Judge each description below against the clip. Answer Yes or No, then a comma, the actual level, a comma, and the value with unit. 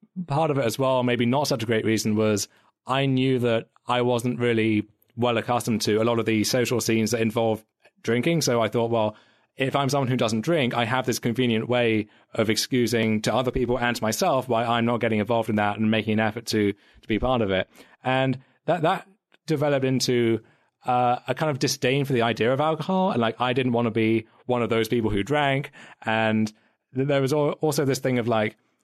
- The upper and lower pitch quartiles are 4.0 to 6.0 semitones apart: No, average, 2.8 semitones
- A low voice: Yes, low, 120 Hz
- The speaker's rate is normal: No, fast, 220 wpm